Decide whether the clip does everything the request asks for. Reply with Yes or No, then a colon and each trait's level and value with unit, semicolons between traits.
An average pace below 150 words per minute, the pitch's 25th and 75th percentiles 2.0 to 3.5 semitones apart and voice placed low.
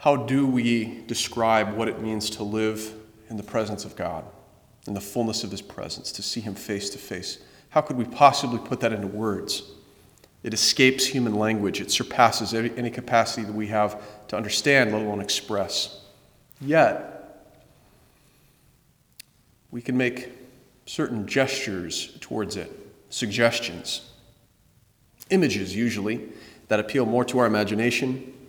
Yes: average, 140 wpm; average, 2.8 semitones; low, 115 Hz